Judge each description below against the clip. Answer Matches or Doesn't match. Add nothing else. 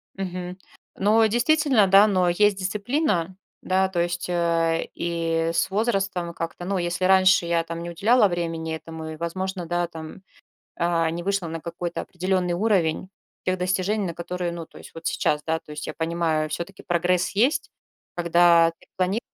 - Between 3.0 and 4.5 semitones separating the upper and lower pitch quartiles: Doesn't match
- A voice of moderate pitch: Matches